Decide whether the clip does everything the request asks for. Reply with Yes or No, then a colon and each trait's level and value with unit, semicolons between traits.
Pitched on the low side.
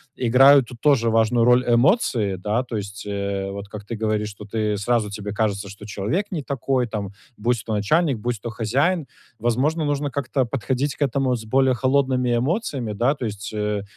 Yes: low, 120 Hz